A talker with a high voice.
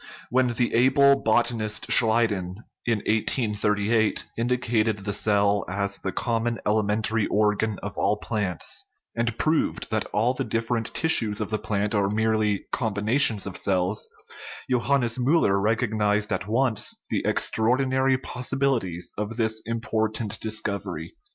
No: low, 110 Hz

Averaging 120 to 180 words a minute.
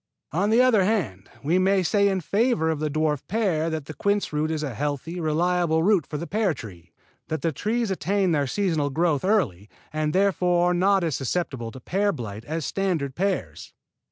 No: average, 195 wpm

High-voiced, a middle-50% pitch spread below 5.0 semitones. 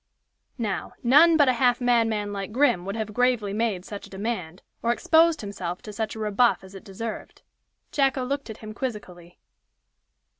Yes: high, 220 Hz; average, 3.9 semitones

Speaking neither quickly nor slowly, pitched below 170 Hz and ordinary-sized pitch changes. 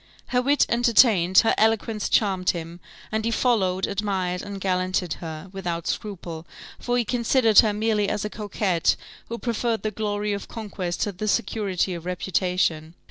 No: average, 160 wpm; high, 200 Hz; average, 3.4 semitones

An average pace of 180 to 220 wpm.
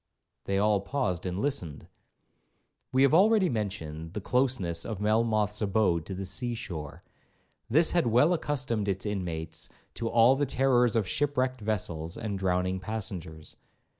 No: average, 145 wpm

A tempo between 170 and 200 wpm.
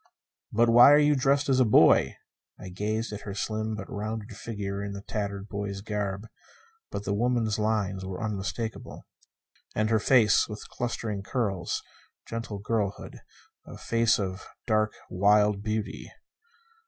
No: average, 140 wpm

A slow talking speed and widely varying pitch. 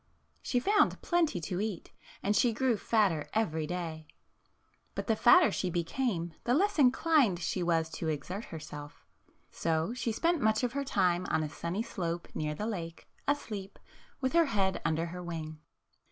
No: average, 170 wpm; wide, 6.7 semitones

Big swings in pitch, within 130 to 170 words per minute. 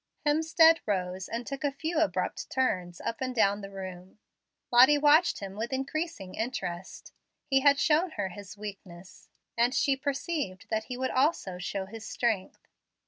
Yes: wide, 6.9 semitones; average, 160 wpm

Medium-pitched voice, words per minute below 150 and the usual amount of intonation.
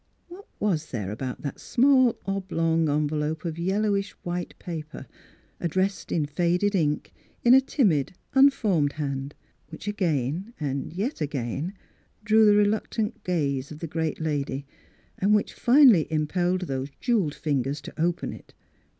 No: medium, 170 Hz; average, 140 wpm; wide, 5.7 semitones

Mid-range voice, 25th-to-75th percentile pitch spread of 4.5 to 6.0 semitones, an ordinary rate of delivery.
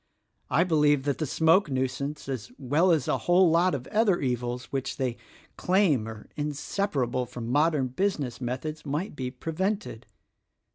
Yes: medium, 145 Hz; average, 4.8 semitones; average, 150 wpm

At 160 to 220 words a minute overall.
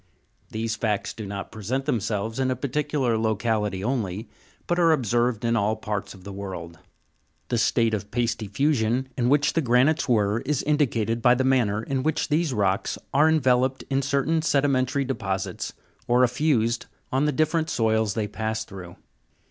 Yes: average, 165 wpm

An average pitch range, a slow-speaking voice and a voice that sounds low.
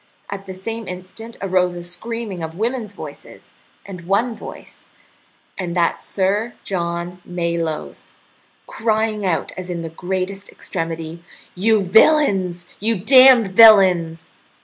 No: average, 3.9 semitones; slow, 125 wpm; medium, 185 Hz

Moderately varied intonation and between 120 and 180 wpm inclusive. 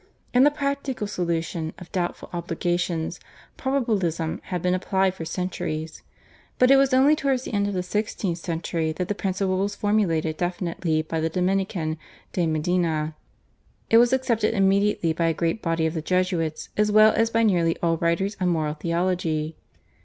Yes: average, 4.0 semitones; average, 170 wpm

